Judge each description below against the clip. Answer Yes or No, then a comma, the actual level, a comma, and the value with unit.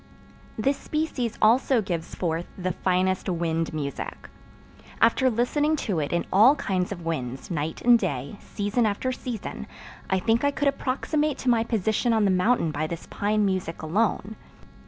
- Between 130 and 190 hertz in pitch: No, high, 205 Hz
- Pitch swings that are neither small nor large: No, wide, 6.0 semitones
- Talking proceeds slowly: No, average, 160 wpm